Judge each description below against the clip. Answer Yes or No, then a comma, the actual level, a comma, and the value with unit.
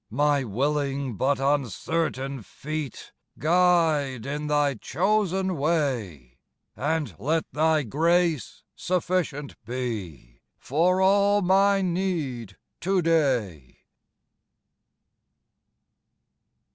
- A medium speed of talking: No, slow, 80 wpm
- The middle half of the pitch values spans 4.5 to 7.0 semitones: Yes, average, 5.2 semitones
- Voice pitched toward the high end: No, medium, 150 Hz